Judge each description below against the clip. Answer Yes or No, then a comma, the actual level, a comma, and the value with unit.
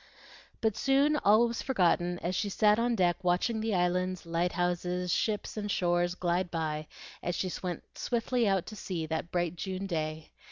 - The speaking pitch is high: No, medium, 180 Hz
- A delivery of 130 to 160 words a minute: No, average, 170 wpm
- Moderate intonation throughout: Yes, average, 3.3 semitones